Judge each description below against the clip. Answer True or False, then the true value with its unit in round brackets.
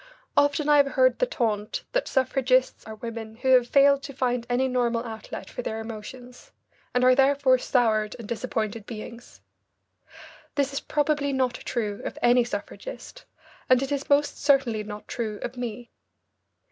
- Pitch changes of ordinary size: True (3.3 semitones)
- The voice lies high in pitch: True (250 Hz)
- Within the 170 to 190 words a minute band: False (160 wpm)